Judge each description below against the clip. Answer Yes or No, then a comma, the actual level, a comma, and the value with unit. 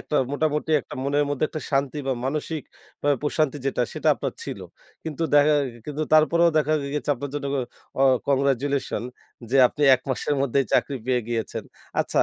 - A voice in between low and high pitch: Yes, medium, 145 Hz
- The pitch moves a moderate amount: No, narrow, 1.9 semitones